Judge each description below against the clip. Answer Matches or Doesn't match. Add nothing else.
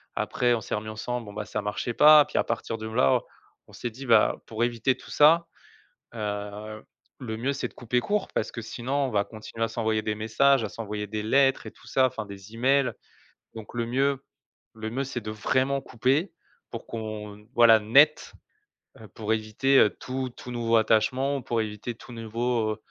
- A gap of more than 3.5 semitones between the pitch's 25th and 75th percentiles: Doesn't match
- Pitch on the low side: Matches